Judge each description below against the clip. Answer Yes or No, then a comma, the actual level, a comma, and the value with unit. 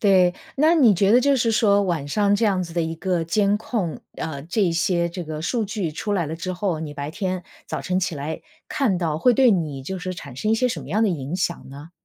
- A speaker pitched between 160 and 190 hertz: Yes, medium, 185 Hz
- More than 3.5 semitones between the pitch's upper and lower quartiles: Yes, average, 4.4 semitones